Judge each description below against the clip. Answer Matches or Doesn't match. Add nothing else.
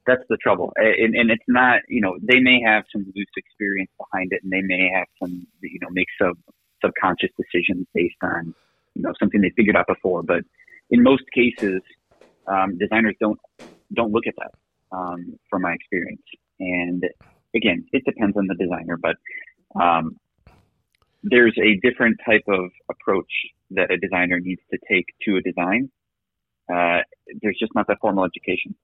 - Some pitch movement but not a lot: Matches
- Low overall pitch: Matches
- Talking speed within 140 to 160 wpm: Doesn't match